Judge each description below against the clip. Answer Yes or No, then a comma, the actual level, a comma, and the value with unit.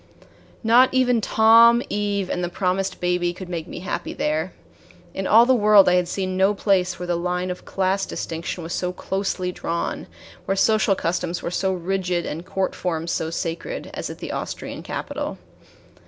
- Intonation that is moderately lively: No, narrow, 2.2 semitones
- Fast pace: No, average, 180 wpm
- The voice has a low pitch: No, medium, 185 Hz